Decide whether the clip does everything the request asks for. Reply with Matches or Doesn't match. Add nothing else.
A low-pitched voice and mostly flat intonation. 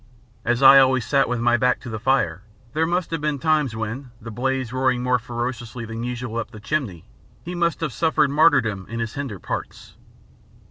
Doesn't match